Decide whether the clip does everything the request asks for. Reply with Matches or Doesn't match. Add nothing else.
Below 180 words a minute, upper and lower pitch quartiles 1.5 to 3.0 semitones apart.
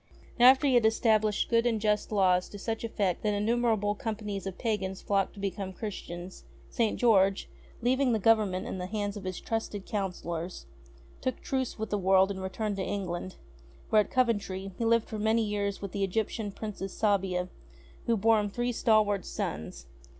Doesn't match